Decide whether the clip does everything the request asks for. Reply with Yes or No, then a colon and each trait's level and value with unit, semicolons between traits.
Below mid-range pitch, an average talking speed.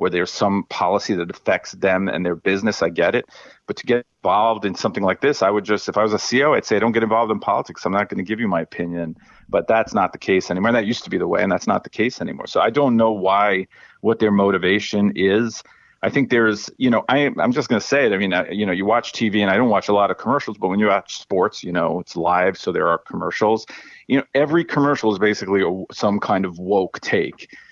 No: low, 105 Hz; fast, 270 wpm